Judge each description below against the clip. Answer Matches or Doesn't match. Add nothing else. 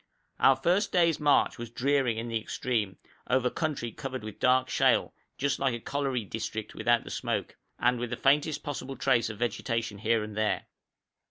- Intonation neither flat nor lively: Matches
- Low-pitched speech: Matches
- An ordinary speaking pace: Matches